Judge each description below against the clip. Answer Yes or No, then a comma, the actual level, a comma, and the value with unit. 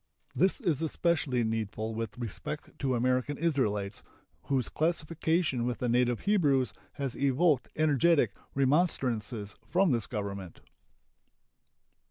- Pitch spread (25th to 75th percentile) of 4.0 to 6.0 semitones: Yes, wide, 5.4 semitones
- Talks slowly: Yes, slow, 110 wpm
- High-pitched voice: No, low, 130 Hz